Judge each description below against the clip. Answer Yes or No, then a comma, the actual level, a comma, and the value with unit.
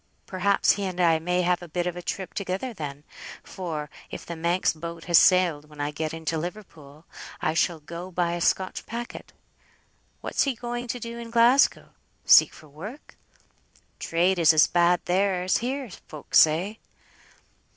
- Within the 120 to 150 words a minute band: No, average, 170 wpm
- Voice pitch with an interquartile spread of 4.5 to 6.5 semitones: No, average, 3.6 semitones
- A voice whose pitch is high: No, medium, 175 Hz